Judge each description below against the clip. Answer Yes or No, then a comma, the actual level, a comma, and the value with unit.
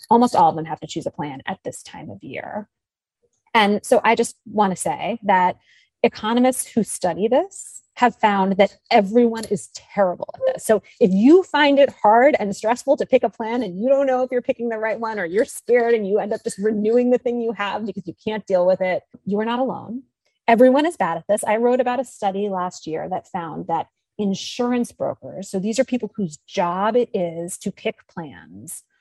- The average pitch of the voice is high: Yes, high, 220 Hz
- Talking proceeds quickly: Yes, fast, 220 wpm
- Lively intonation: No, average, 3.5 semitones